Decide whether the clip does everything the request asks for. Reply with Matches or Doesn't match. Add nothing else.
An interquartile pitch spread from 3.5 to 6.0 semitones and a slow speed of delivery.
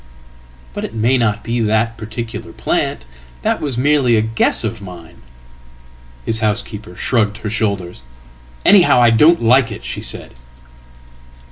Matches